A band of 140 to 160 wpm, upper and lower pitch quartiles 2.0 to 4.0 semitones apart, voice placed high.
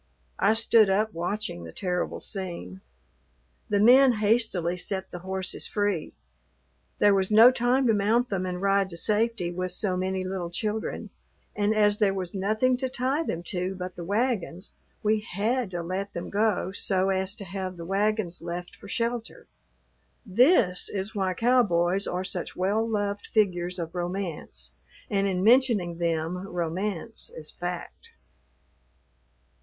Yes: average, 150 wpm; average, 3.3 semitones; high, 195 Hz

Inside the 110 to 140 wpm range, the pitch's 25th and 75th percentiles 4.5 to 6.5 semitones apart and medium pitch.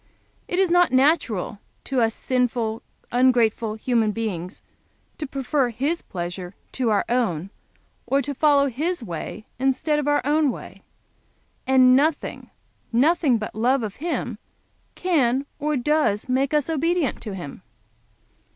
No: slow, 135 wpm; average, 5.0 semitones; very high, 255 Hz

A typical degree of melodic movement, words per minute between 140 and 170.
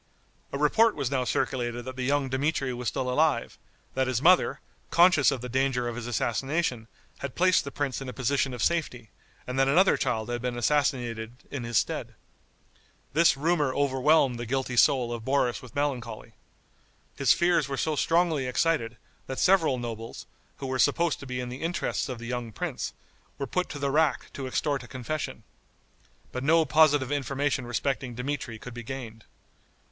No: average, 3.1 semitones; average, 180 wpm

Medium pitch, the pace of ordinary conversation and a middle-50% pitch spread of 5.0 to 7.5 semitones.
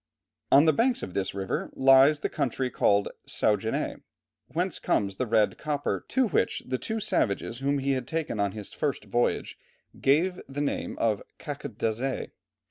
No: low, 130 Hz; average, 160 wpm; average, 5.3 semitones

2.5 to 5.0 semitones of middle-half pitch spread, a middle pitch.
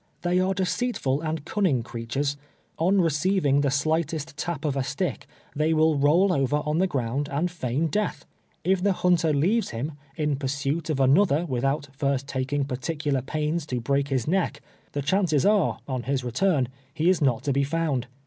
Yes: average, 3.8 semitones; medium, 150 Hz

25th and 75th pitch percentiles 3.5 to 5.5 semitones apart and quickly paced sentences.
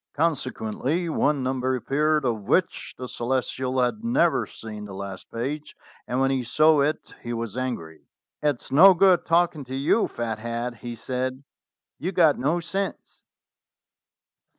No: average, 4.7 semitones; average, 150 wpm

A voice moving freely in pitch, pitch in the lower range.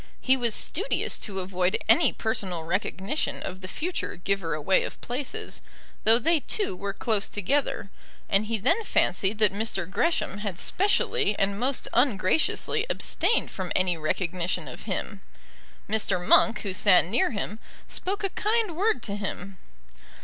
No: wide, 6.5 semitones; high, 205 Hz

